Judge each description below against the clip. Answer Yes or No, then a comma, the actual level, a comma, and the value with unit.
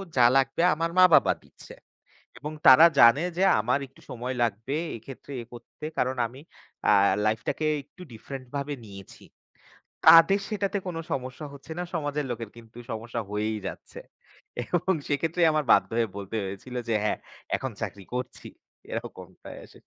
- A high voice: No, low, 130 Hz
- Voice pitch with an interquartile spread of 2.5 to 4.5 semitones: No, average, 5.1 semitones